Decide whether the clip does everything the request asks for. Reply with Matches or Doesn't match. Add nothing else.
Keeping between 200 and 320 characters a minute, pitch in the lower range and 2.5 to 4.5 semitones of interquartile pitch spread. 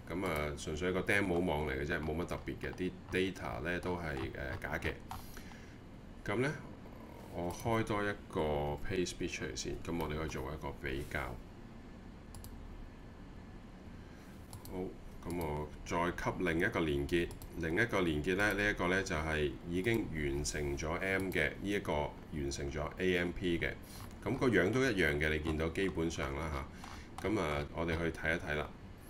Matches